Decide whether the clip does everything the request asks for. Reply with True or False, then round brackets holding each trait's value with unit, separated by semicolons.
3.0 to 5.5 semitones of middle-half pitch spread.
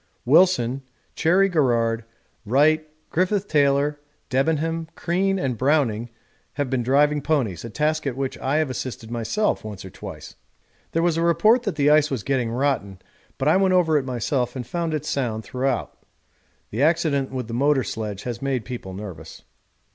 True (4.7 semitones)